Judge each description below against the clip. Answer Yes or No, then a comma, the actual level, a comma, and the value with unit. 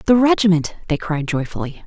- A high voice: No, medium, 175 Hz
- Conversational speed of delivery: Yes, average, 160 wpm